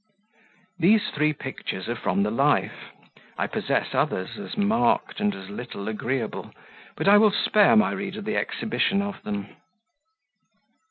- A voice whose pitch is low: No, high, 190 Hz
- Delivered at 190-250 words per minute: No, average, 145 wpm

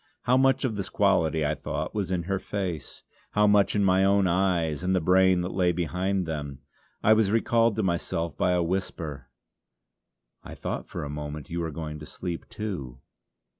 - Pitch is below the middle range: Yes, very low, 90 Hz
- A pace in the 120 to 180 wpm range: No, average, 190 wpm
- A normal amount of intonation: Yes, average, 3.7 semitones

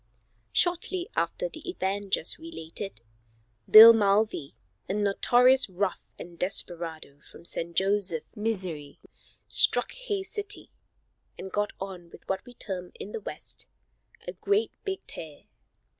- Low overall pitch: No, high, 200 Hz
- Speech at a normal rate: No, slow, 125 wpm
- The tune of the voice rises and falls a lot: Yes, wide, 7.0 semitones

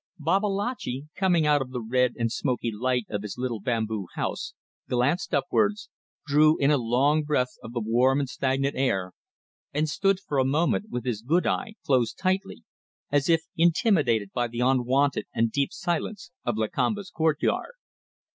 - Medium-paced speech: Yes, average, 165 wpm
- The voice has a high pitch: No, low, 135 Hz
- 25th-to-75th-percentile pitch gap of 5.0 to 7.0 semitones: Yes, average, 5.3 semitones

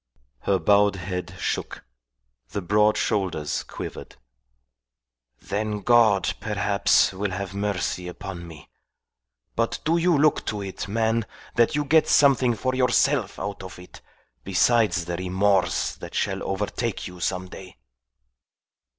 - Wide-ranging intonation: No, average, 3.7 semitones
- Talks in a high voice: No, low, 100 Hz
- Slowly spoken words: Yes, slow, 130 wpm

